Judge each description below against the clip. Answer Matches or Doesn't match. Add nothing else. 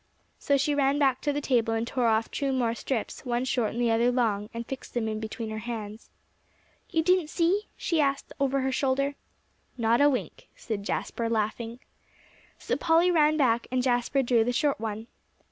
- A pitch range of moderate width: Matches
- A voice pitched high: Matches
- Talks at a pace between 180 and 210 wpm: Matches